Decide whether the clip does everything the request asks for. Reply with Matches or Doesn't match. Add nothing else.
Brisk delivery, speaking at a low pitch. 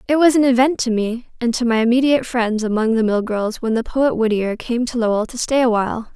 Doesn't match